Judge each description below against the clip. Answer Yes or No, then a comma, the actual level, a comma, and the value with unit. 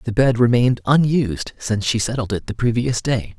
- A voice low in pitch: Yes, low, 115 Hz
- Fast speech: No, average, 195 wpm